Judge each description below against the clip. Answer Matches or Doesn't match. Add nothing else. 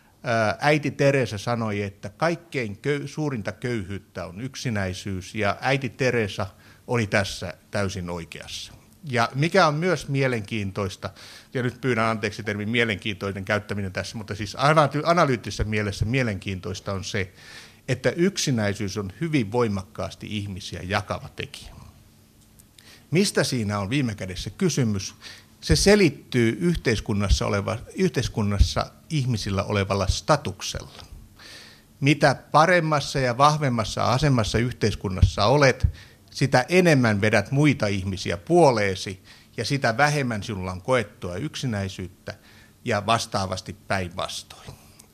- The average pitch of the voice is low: Matches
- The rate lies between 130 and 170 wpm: Doesn't match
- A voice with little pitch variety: Doesn't match